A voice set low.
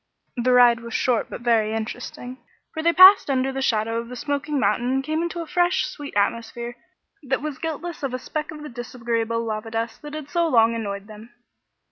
No: very high, 250 Hz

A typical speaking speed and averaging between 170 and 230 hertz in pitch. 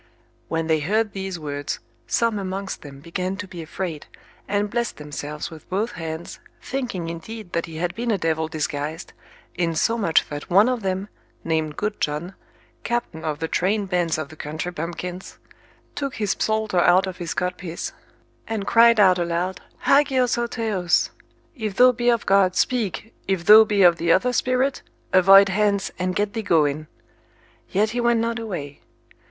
Yes: average, 170 wpm; medium, 185 Hz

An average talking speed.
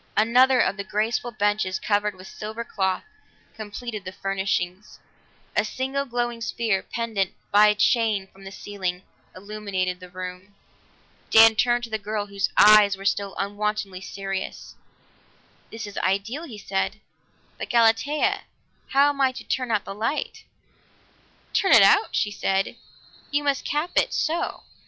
Yes: average, 150 wpm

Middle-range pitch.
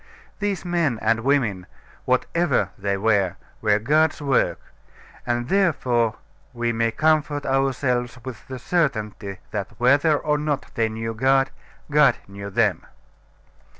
No: low, 125 Hz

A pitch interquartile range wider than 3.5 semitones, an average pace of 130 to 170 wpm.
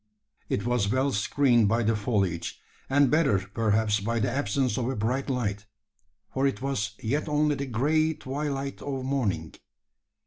Yes: average, 4.6 semitones; average, 160 wpm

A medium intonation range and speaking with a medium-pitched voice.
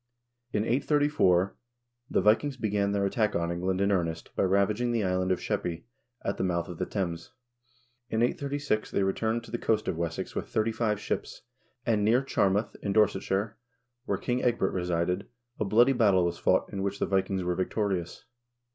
No: average, 3.4 semitones; low, 100 Hz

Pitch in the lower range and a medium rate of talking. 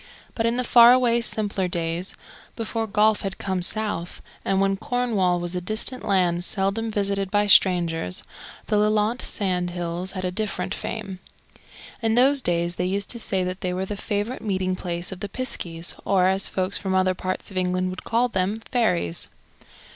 No: high, 195 Hz; average, 180 wpm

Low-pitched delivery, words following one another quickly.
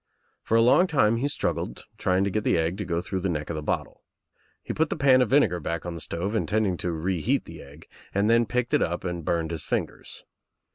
Yes: very low, 95 Hz; fast, 235 wpm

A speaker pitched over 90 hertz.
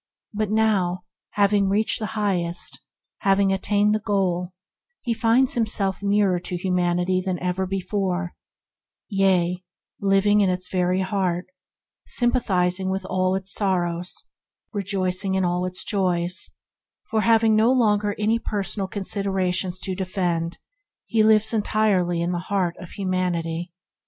Yes: high, 190 Hz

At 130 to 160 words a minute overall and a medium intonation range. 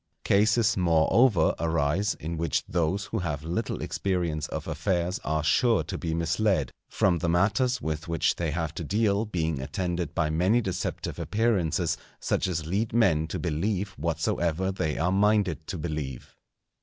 Yes: average, 155 wpm; average, 3.9 semitones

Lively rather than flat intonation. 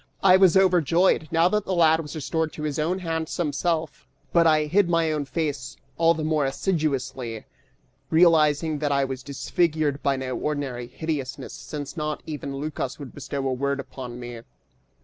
No: average, 3.1 semitones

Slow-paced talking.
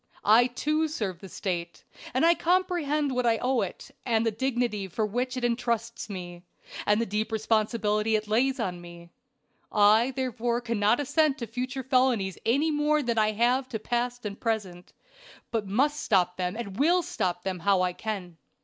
No: average, 175 wpm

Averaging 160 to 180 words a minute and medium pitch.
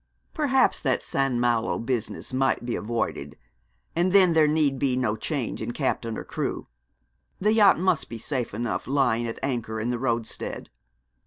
No: average, 165 wpm; low, 130 Hz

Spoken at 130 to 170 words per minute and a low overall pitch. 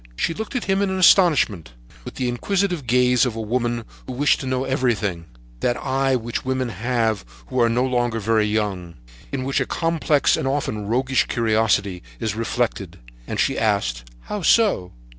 Yes: average, 165 wpm; low, 120 Hz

